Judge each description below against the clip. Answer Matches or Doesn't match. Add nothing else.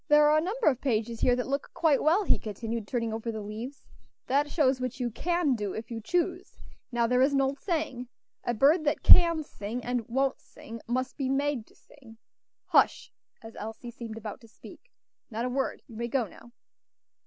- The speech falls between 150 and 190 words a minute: Doesn't match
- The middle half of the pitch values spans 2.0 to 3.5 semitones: Doesn't match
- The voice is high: Matches